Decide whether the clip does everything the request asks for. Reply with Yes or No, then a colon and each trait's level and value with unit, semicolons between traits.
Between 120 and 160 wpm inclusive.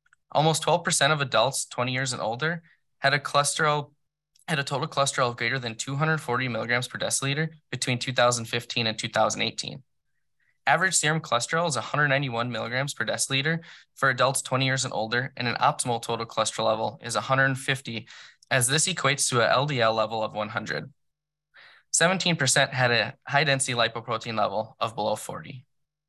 Yes: average, 150 wpm